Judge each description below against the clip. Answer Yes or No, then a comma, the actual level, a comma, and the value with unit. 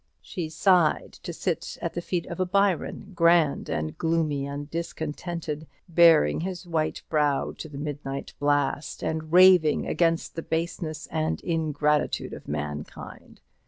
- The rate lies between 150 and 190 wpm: No, average, 140 wpm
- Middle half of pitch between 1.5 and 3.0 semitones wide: Yes, average, 2.7 semitones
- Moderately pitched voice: Yes, medium, 160 Hz